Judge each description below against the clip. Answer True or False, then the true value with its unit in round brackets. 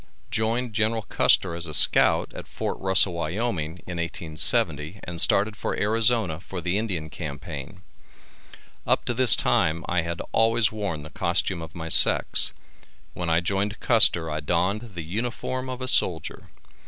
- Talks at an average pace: True (155 wpm)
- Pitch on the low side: True (90 Hz)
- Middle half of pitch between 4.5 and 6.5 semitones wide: True (5.1 semitones)